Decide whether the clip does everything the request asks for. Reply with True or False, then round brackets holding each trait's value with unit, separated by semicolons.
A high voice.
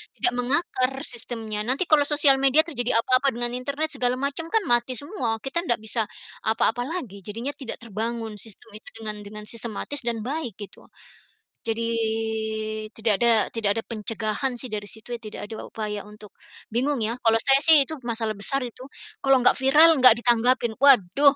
True (240 Hz)